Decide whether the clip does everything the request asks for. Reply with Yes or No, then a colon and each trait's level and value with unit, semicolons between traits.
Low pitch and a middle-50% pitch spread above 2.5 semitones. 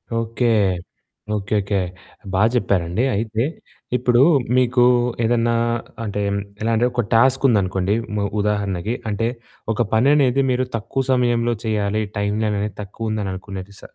Yes: low, 110 Hz; average, 2.9 semitones